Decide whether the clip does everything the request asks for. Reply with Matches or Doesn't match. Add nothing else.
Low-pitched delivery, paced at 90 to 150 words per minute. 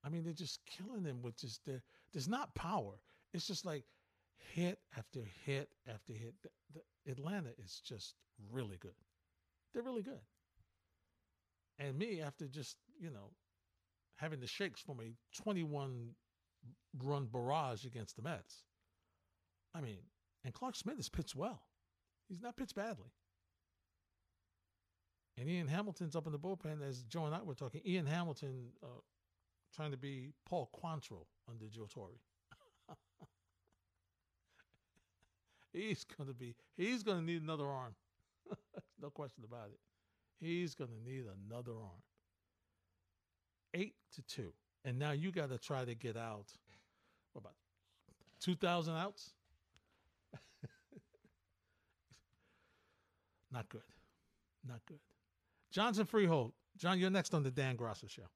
Matches